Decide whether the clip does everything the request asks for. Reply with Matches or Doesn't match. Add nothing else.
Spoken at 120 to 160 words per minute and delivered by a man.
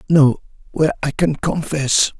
Matches